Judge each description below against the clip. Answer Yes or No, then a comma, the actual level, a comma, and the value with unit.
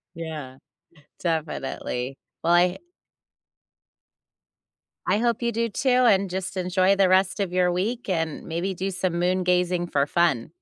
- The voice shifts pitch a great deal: No, narrow, 2.5 semitones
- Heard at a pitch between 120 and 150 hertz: No, medium, 180 Hz